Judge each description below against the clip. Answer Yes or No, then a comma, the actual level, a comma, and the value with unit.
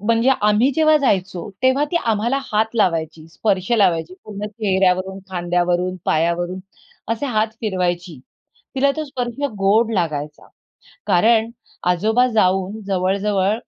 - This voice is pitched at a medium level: No, high, 200 Hz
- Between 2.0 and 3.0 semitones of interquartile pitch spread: No, average, 4.0 semitones